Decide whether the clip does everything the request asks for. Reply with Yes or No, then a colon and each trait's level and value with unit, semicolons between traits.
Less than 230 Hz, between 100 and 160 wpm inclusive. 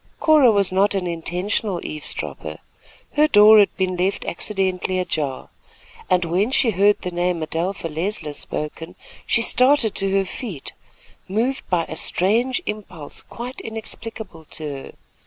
Yes: high, 190 Hz; average, 140 wpm